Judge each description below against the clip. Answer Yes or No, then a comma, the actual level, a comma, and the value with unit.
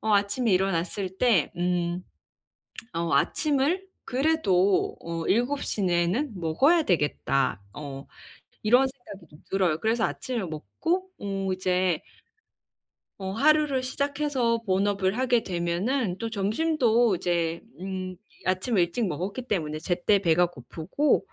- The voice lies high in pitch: Yes, high, 195 Hz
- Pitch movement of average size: No, wide, 6.1 semitones